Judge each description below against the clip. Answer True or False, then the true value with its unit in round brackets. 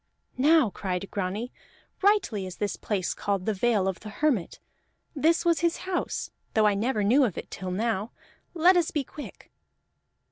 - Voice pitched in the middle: False (220 Hz)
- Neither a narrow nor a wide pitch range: False (7.6 semitones)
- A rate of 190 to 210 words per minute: False (170 wpm)